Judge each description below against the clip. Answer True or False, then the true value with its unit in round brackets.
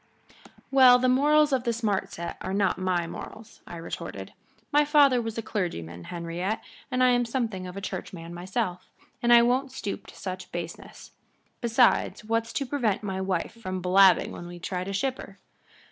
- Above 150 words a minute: True (175 wpm)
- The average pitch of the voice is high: True (205 Hz)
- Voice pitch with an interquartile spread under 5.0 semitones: False (5.3 semitones)